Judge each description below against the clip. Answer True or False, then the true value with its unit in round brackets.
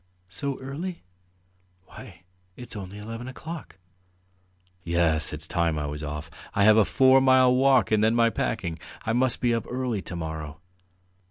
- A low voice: True (110 Hz)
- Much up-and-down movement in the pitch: True (7.6 semitones)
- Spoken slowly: False (160 wpm)